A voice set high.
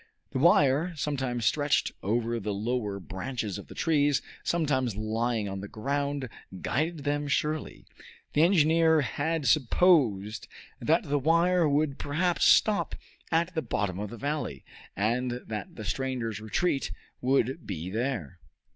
No: low, 135 Hz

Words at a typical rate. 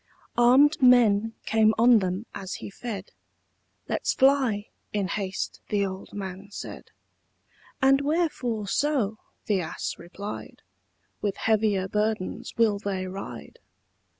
No: slow, 120 wpm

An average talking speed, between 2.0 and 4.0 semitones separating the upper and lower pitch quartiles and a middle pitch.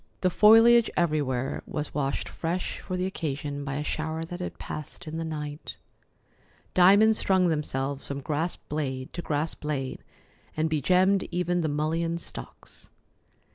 Yes: average, 145 wpm; average, 3.5 semitones; medium, 160 Hz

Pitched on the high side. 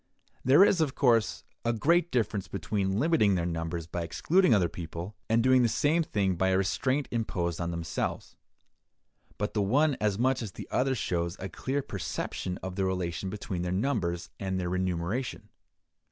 No: low, 100 Hz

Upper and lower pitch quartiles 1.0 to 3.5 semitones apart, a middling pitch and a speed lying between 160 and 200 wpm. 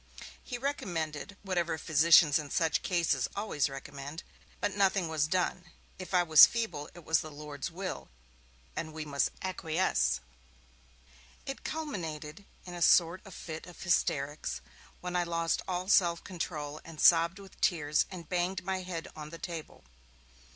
No: average, 3.2 semitones; medium, 170 Hz; average, 150 wpm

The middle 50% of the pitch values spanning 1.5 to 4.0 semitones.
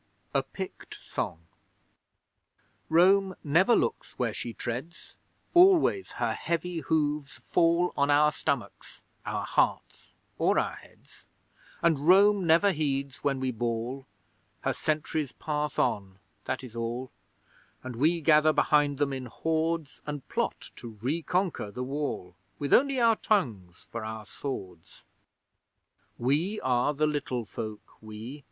No: average, 5.2 semitones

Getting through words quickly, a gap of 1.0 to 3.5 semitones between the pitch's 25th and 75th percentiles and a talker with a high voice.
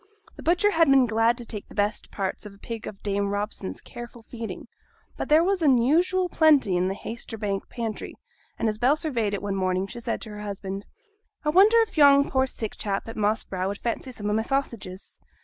No: fast, 215 wpm; average, 5.3 semitones; high, 225 Hz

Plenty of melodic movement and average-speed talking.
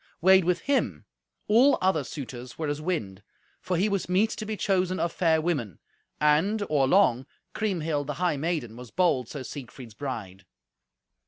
Yes: wide, 6.0 semitones; average, 165 wpm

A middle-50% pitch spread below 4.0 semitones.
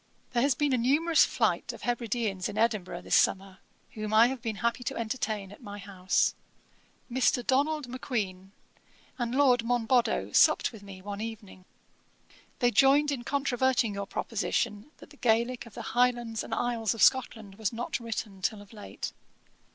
Yes: average, 3.4 semitones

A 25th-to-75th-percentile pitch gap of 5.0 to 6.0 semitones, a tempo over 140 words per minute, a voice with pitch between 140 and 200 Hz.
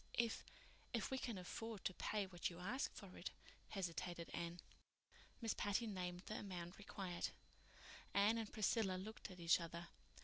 No: average, 3.6 semitones; average, 150 wpm; high, 190 Hz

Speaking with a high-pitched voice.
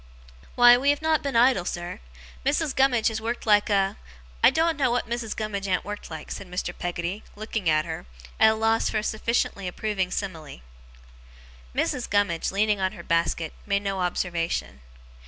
Yes: high, 205 Hz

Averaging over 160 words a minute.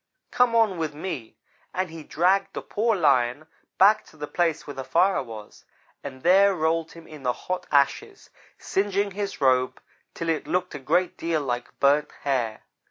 Yes: average, 175 wpm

